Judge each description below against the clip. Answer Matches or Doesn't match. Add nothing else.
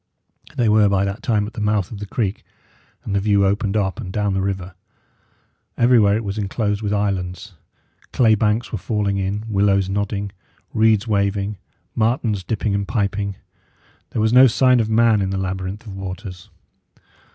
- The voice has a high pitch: Doesn't match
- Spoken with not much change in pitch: Matches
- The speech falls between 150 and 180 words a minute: Matches